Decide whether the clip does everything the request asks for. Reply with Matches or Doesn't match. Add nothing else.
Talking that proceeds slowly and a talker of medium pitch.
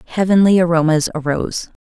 Matches